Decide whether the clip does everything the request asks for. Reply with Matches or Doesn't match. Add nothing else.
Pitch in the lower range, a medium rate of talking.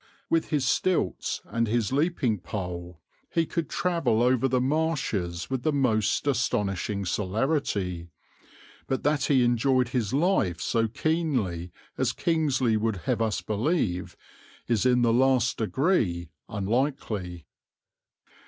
Doesn't match